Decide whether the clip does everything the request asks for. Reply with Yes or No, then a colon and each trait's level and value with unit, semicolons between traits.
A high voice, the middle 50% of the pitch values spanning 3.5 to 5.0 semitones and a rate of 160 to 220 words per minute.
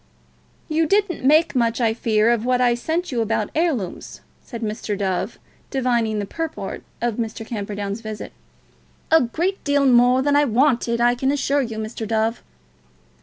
Yes: high, 240 Hz; average, 4.5 semitones; average, 165 wpm